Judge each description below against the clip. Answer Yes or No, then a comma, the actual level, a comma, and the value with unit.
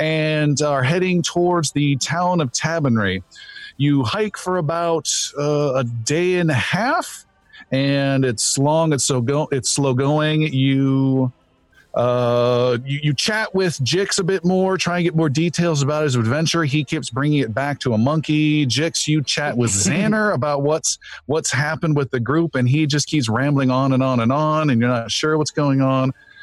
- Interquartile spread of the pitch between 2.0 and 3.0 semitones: No, average, 3.7 semitones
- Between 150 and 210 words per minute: Yes, average, 185 wpm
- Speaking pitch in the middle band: Yes, medium, 145 Hz